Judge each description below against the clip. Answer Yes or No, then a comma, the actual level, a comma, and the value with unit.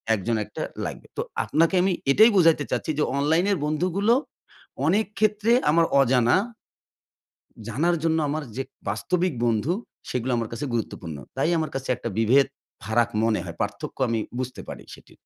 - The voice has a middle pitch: Yes, medium, 145 Hz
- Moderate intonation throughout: No, wide, 6.7 semitones